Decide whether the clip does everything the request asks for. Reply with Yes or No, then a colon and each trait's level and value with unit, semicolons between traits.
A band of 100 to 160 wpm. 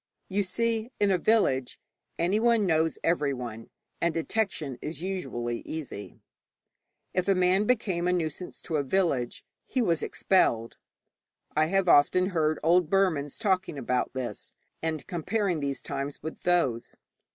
Yes: average, 140 wpm